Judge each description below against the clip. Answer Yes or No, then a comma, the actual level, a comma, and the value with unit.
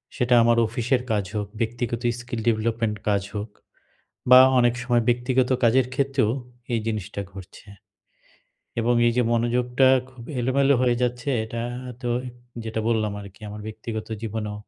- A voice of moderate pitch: No, low, 115 Hz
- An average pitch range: No, narrow, 2.1 semitones